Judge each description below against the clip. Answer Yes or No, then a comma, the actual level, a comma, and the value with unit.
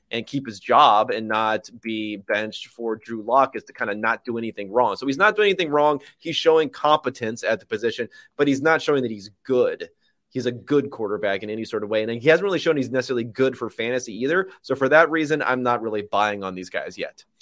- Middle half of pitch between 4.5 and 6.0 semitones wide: Yes, average, 5.2 semitones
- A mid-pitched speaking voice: No, low, 125 Hz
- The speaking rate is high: Yes, fast, 240 wpm